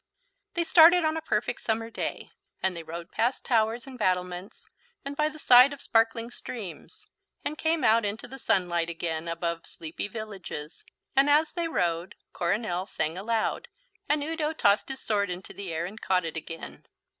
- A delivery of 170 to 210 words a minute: Yes, average, 175 wpm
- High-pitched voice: Yes, high, 215 Hz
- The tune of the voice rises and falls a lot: Yes, wide, 7.4 semitones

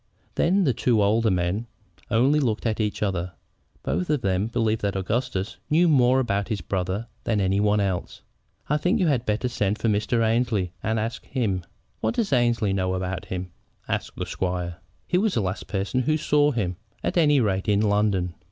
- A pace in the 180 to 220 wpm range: Yes, average, 190 wpm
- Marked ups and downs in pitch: No, average, 4.7 semitones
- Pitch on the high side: No, low, 110 Hz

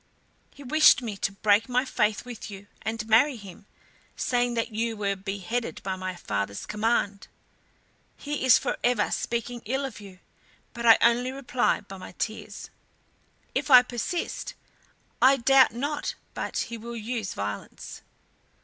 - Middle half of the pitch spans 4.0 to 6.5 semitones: No, average, 3.5 semitones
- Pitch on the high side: Yes, high, 230 Hz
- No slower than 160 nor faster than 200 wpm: No, average, 150 wpm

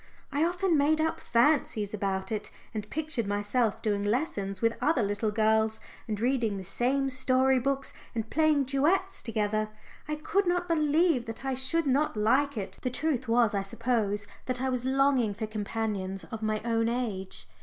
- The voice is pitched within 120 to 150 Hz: No, high, 235 Hz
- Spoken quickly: No, average, 175 wpm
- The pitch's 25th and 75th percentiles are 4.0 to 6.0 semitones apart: Yes, average, 4.9 semitones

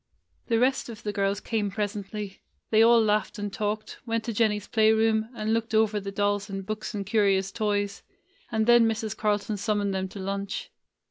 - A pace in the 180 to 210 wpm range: Yes, average, 190 wpm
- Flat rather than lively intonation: Yes, narrow, 1.7 semitones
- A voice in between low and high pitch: No, high, 210 Hz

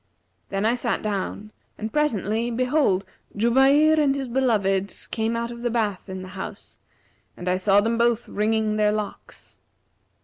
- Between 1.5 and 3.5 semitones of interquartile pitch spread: Yes, average, 3.0 semitones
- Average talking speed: Yes, average, 160 wpm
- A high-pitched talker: Yes, high, 220 Hz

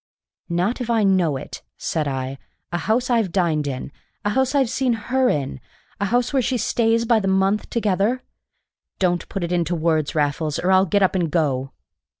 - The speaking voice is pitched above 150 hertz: Yes, high, 190 Hz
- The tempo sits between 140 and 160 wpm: No, average, 190 wpm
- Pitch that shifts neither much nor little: No, wide, 6.4 semitones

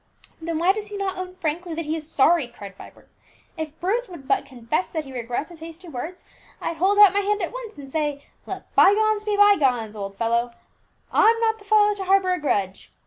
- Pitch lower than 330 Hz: No, very high, 335 Hz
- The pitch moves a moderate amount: No, wide, 6.7 semitones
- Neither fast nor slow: No, fast, 225 wpm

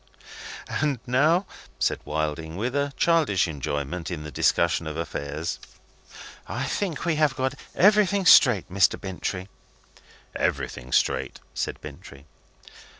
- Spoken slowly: Yes, slow, 120 wpm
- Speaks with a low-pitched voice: Yes, very low, 95 Hz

